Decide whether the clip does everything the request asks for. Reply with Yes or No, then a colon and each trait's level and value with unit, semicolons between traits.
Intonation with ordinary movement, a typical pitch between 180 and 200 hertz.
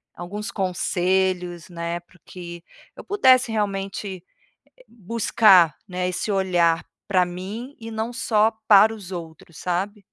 Yes: average, 3.4 semitones; high, 190 Hz